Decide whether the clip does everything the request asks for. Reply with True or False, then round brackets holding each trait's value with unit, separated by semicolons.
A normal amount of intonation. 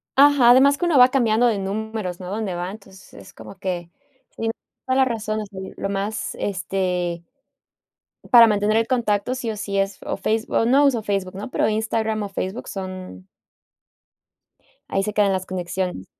True (3.2 semitones)